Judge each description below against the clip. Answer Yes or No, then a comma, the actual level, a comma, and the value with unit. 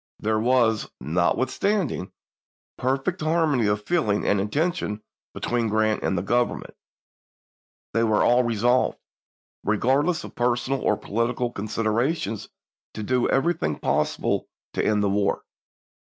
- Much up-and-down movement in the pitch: No, average, 3.9 semitones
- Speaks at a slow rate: Yes, slow, 120 wpm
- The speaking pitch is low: Yes, low, 115 Hz